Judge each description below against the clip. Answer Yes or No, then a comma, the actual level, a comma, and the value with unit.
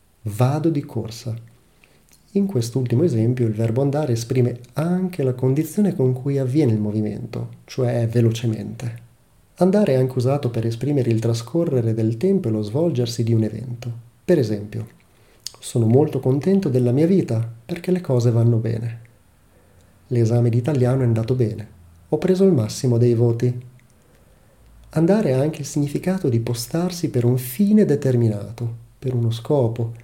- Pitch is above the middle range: No, low, 120 Hz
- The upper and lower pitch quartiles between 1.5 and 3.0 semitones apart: No, average, 3.5 semitones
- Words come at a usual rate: Yes, average, 150 wpm